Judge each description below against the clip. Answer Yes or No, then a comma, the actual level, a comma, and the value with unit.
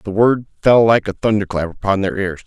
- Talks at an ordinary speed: No, fast, 220 wpm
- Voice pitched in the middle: No, low, 100 Hz